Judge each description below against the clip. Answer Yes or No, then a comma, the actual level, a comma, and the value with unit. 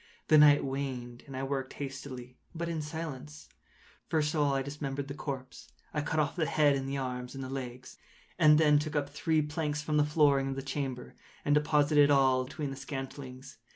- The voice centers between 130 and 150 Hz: Yes, medium, 140 Hz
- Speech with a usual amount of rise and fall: No, narrow, 2.0 semitones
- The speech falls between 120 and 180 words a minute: No, average, 200 wpm